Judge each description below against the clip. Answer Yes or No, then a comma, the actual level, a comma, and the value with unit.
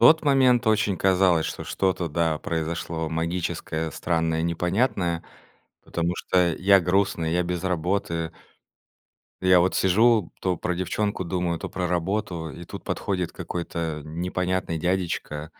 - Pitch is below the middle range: Yes, very low, 90 Hz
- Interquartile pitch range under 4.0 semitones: Yes, narrow, 2.4 semitones